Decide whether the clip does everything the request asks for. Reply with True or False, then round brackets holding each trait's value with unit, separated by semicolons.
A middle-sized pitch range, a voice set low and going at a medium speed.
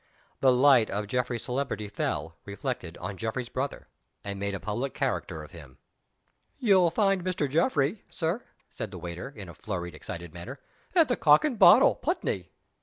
False (7.5 semitones; 120 Hz; 170 wpm)